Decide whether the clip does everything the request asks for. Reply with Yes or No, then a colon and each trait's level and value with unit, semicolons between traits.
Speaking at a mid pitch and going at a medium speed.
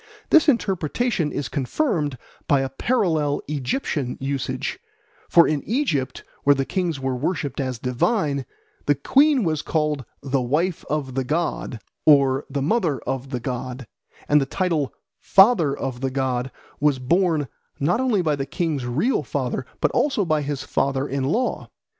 Yes: medium, 145 Hz; average, 155 wpm